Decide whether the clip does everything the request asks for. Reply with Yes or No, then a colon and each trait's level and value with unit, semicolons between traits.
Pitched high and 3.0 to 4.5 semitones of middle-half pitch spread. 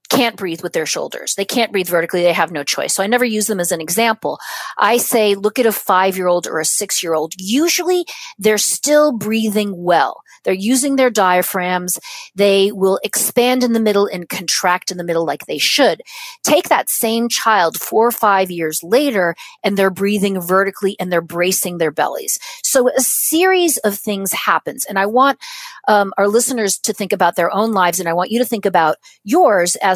No: high, 205 Hz; average, 5.2 semitones